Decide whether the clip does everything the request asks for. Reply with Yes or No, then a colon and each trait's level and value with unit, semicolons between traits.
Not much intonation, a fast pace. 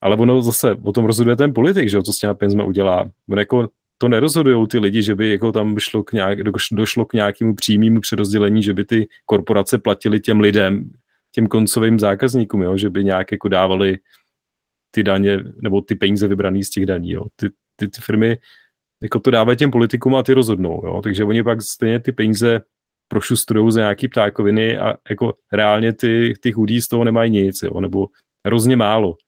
Yes: narrow, 2.3 semitones; fast, 195 wpm